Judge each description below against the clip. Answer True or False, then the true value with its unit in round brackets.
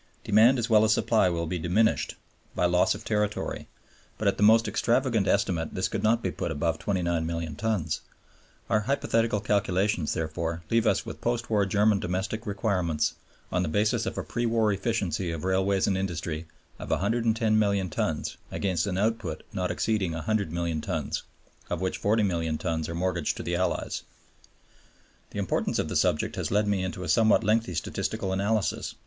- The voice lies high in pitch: False (95 Hz)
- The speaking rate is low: False (170 wpm)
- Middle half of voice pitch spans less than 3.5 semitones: False (4.1 semitones)